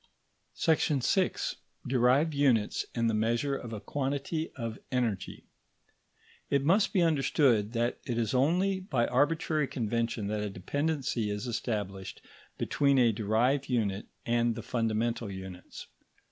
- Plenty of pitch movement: No, average, 4.4 semitones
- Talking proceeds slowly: Yes, slow, 130 wpm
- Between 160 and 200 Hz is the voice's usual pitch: No, low, 120 Hz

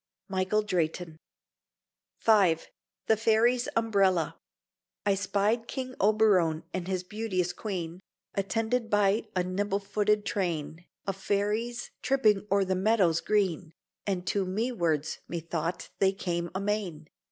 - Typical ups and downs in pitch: Yes, average, 3.2 semitones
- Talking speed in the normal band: No, slow, 120 wpm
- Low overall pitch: No, high, 195 Hz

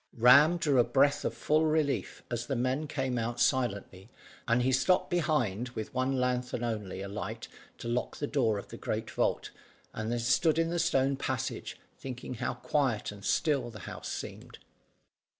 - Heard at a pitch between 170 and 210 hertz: No, low, 125 Hz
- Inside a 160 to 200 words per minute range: Yes, average, 175 wpm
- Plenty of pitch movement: No, average, 3.7 semitones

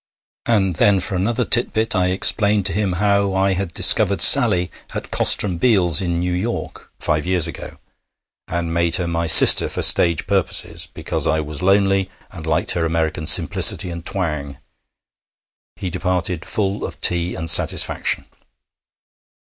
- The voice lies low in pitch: Yes, very low, 90 Hz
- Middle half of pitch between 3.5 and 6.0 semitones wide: No, average, 2.8 semitones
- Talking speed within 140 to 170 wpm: Yes, average, 155 wpm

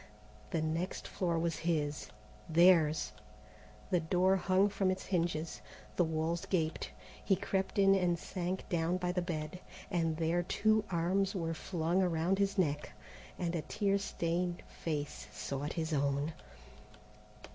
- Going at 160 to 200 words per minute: No, average, 140 wpm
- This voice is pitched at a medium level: Yes, medium, 175 Hz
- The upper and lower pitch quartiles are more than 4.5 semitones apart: No, narrow, 2.6 semitones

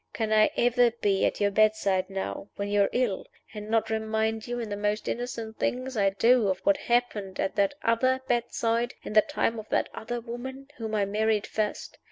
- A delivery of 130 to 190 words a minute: No, fast, 205 wpm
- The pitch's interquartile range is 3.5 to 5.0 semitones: No, narrow, 2.6 semitones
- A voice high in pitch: Yes, high, 220 Hz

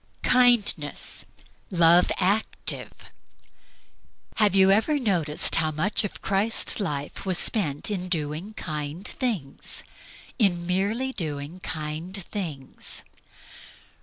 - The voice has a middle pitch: Yes, medium, 180 Hz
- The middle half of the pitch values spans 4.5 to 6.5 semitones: Yes, average, 5.0 semitones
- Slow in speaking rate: Yes, slow, 100 wpm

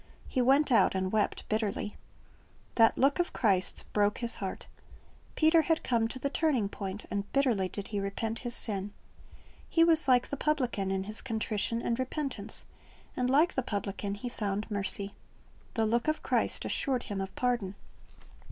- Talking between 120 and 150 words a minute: No, average, 170 wpm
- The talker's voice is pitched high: Yes, high, 225 Hz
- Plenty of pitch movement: No, average, 4.5 semitones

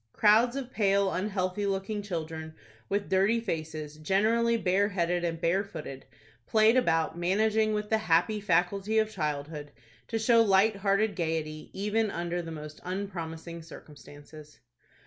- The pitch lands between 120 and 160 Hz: No, high, 190 Hz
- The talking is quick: No, average, 140 wpm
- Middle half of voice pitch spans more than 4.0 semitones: Yes, average, 4.6 semitones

